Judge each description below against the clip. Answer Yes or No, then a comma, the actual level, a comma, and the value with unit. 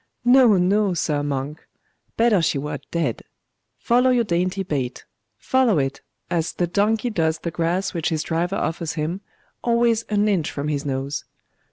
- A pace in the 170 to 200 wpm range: No, average, 160 wpm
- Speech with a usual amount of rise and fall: No, wide, 5.8 semitones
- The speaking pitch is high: No, medium, 175 Hz